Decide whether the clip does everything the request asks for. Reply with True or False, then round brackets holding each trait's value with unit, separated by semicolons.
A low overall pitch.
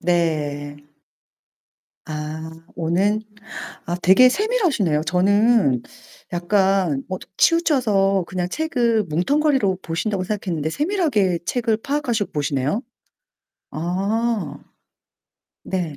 False (190 Hz)